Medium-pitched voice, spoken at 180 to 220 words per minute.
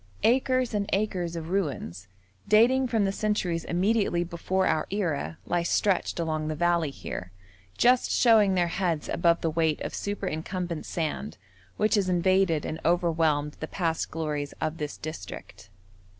No: medium, 175 Hz; average, 150 wpm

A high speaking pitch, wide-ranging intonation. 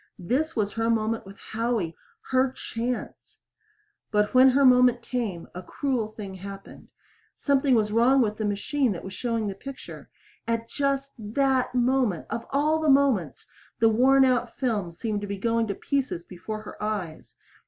No: high, 230 Hz; average, 4.1 semitones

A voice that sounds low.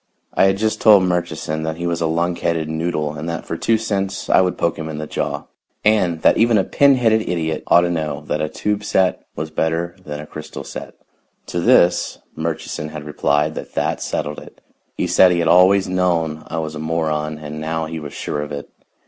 Yes: very low, 80 Hz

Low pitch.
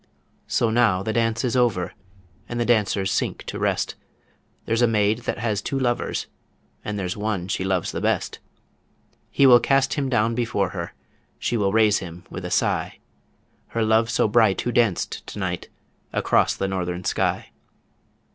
Yes: low, 110 Hz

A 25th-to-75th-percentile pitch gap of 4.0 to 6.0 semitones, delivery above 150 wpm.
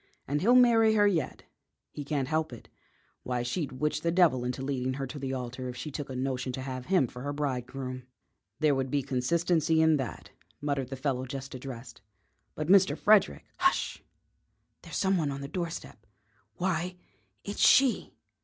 Yes: average, 4.7 semitones; average, 180 wpm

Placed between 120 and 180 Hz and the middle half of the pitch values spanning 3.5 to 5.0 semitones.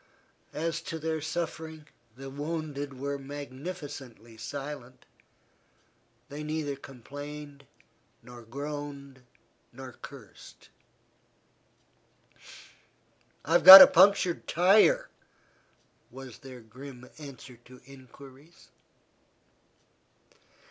No: medium, 140 Hz; average, 3.0 semitones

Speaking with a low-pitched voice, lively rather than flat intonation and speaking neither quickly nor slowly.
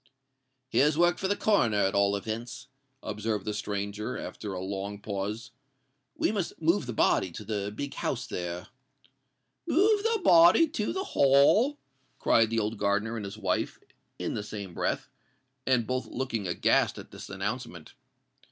Yes: low, 110 Hz; wide, 6.7 semitones; average, 160 wpm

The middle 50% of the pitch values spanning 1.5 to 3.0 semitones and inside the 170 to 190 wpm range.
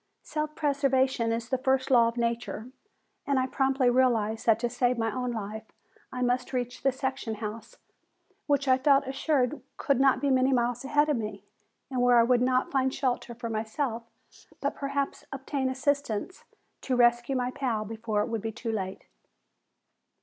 Yes: narrow, 2.6 semitones; average, 180 wpm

